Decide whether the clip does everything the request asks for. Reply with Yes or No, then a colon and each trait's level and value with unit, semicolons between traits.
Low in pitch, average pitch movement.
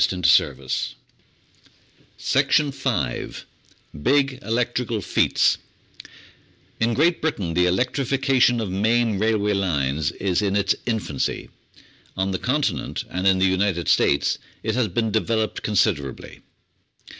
Yes: low, 105 Hz; average, 4.8 semitones